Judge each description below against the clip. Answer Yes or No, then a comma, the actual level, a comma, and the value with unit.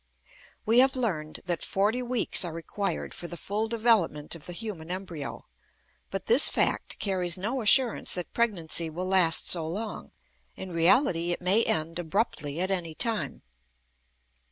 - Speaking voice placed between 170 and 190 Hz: Yes, medium, 185 Hz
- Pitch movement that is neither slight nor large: Yes, average, 5.0 semitones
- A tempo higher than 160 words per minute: No, average, 155 wpm